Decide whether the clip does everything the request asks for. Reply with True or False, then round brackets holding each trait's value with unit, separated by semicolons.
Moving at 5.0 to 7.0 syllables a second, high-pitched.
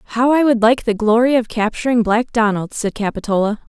True (5.4 syllables/s; 225 Hz)